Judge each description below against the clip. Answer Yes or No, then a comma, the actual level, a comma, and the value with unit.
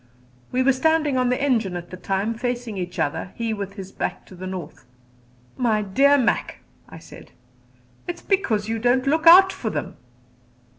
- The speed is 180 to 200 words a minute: Yes, average, 185 wpm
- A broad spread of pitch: Yes, wide, 5.7 semitones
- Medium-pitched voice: No, high, 230 Hz